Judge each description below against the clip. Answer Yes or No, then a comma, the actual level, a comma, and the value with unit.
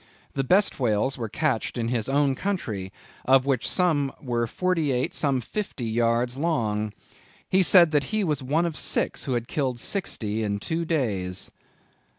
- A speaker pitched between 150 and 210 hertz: No, low, 130 Hz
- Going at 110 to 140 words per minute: No, average, 165 wpm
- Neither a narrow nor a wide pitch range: No, wide, 5.7 semitones